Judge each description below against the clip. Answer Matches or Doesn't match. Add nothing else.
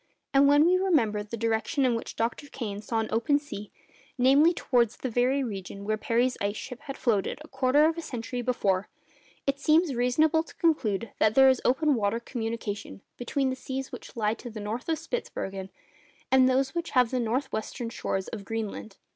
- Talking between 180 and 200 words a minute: Matches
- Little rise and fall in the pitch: Doesn't match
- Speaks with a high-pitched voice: Matches